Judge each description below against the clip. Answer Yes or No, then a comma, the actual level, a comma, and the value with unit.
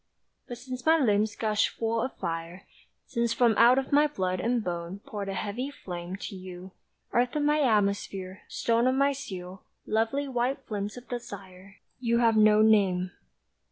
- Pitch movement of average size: Yes, average, 4.5 semitones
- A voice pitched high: Yes, high, 220 Hz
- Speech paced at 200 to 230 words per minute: No, average, 170 wpm